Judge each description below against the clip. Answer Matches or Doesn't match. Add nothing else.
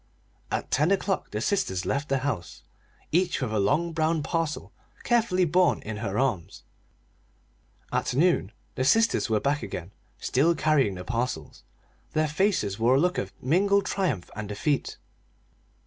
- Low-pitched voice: Doesn't match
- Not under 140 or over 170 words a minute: Matches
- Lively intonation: Matches